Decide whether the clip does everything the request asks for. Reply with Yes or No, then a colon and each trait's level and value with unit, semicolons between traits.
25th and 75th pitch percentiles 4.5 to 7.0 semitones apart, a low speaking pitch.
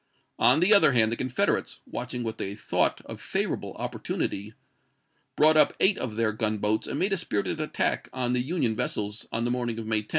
Yes: average, 4.9 semitones; low, 120 Hz